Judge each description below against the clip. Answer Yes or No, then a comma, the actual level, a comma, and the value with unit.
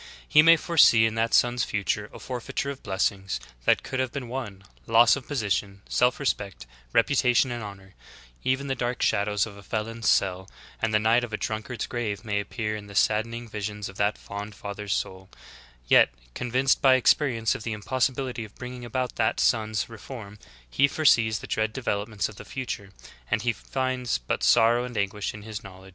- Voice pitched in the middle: No, low, 110 Hz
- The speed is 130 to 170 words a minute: No, average, 195 wpm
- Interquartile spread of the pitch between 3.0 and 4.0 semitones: Yes, average, 3.3 semitones